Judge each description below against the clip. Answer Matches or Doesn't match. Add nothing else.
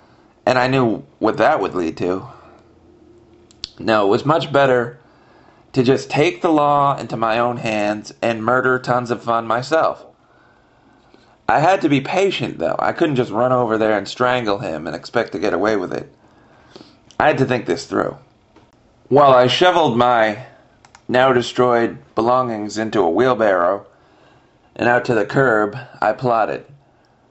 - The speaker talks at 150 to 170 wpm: Matches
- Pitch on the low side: Matches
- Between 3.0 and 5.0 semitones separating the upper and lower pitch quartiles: Doesn't match